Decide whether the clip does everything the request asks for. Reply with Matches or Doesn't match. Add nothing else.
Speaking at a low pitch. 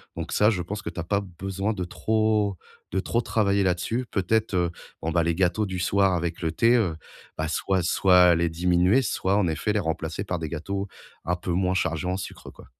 Matches